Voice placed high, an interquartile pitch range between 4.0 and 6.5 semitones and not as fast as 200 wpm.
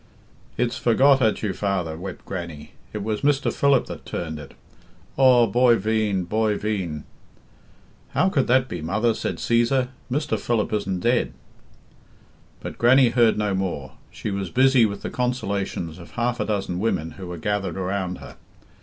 No: low, 105 Hz; average, 4.7 semitones; average, 165 wpm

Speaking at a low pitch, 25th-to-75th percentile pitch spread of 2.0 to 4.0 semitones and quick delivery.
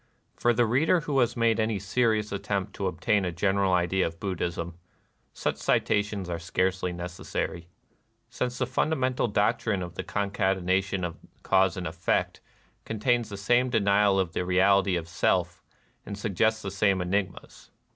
No: low, 100 Hz; average, 3.5 semitones; average, 155 wpm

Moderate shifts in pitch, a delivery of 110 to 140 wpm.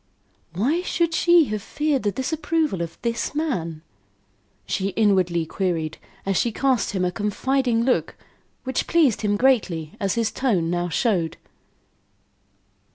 No: wide, 6.9 semitones; slow, 135 wpm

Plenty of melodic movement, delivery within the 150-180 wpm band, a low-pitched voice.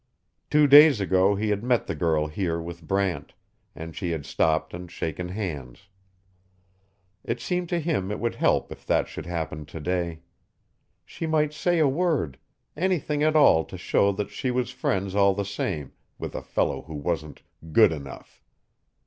Yes: wide, 8.5 semitones; average, 170 wpm; very low, 95 Hz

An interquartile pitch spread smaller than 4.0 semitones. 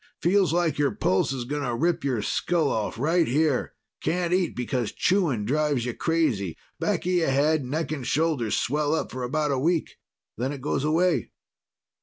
No: average, 4.4 semitones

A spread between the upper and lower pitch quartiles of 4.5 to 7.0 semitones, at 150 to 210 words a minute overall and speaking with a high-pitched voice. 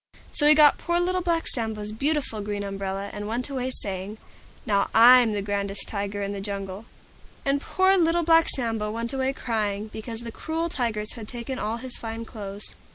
Yes: average, 4.9 semitones; average, 185 wpm; high, 225 Hz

